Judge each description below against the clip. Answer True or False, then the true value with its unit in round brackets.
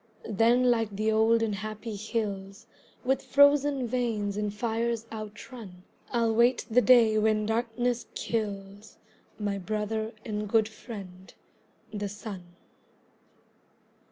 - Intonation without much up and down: True (2.2 semitones)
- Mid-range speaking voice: False (220 Hz)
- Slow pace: True (115 wpm)